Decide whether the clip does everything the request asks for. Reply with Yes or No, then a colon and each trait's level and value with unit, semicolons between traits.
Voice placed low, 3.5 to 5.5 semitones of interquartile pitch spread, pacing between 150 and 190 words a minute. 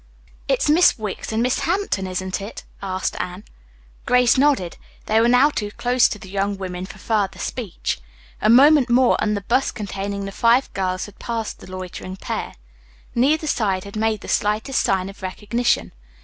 No: high, 210 Hz; average, 4.2 semitones; average, 175 wpm